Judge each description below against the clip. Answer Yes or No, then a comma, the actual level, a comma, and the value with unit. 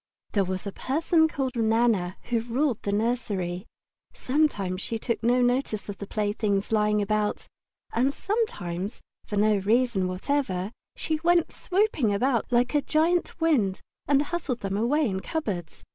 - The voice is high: Yes, high, 230 Hz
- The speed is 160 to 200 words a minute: No, average, 150 wpm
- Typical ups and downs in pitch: No, wide, 5.9 semitones